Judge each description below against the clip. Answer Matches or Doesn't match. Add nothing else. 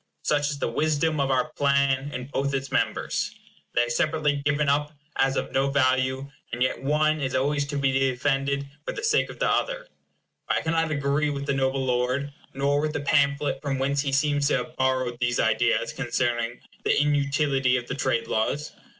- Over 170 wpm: Matches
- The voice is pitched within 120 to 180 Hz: Matches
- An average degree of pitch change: Doesn't match